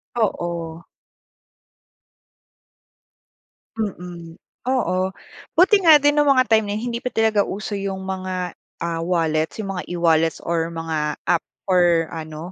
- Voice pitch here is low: No, medium, 180 Hz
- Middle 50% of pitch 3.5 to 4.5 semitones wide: No, average, 4.9 semitones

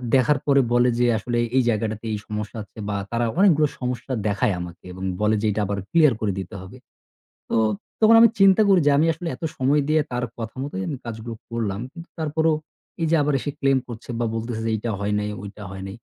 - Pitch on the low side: Yes, low, 120 Hz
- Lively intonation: Yes, wide, 5.7 semitones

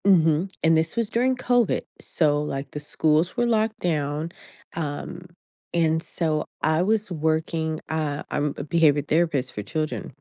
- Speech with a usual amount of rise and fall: Yes, average, 3.1 semitones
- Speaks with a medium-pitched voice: Yes, medium, 160 Hz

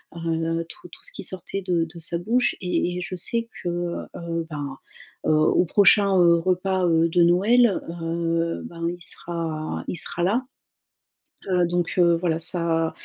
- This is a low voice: No, medium, 170 Hz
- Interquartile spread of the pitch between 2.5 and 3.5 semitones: No, narrow, 1.7 semitones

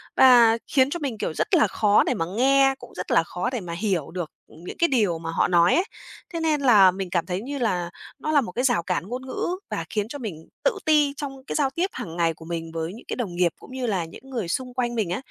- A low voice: No, high, 225 Hz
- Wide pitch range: Yes, wide, 7.4 semitones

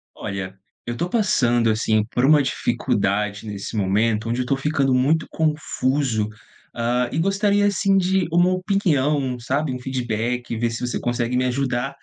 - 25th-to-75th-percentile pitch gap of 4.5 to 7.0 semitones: Yes, average, 4.9 semitones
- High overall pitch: No, low, 125 Hz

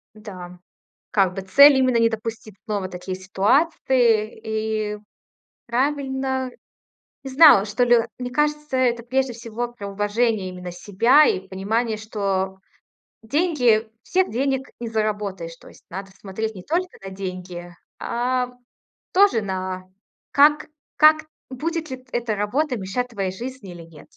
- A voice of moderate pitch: No, high, 225 Hz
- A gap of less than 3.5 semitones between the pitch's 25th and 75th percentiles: No, average, 5.1 semitones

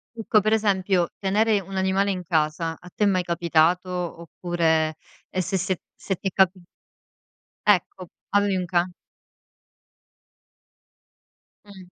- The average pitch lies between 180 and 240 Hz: Yes, medium, 185 Hz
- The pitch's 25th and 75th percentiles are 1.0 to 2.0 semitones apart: No, narrow, 2.4 semitones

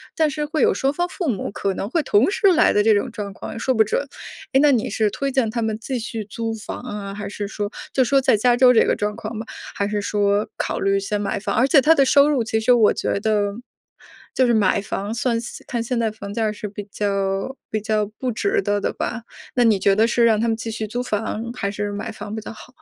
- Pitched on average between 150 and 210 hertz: No, high, 220 Hz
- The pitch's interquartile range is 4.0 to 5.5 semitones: No, average, 3.2 semitones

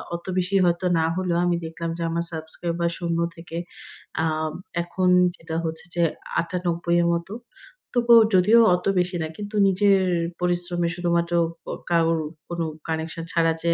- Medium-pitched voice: Yes, medium, 170 Hz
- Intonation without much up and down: Yes, narrow, 1.4 semitones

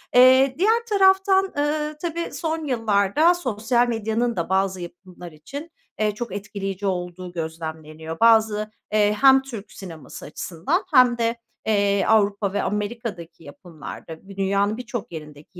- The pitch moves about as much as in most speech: No, wide, 5.9 semitones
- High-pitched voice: Yes, high, 210 Hz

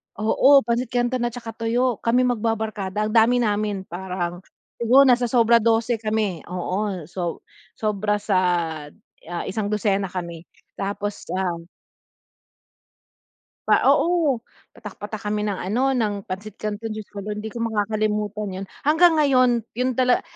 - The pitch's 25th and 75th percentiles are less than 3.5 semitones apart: Yes, average, 3.1 semitones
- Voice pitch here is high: Yes, high, 215 Hz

